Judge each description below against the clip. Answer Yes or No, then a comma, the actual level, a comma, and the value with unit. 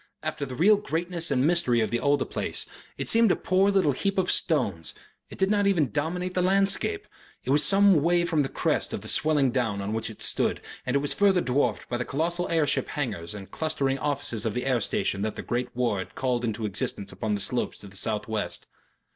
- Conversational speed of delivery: No, fast, 230 wpm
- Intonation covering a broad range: Yes, wide, 7.5 semitones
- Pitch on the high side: No, medium, 140 Hz